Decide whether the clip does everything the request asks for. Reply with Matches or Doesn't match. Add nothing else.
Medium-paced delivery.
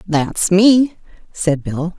Doesn't match